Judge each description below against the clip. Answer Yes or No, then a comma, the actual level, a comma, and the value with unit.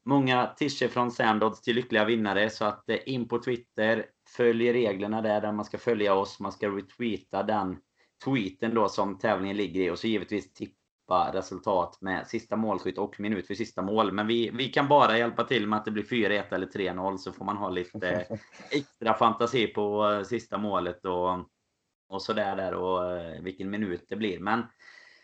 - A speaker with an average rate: Yes, average, 185 wpm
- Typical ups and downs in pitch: Yes, average, 3.2 semitones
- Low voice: Yes, low, 105 Hz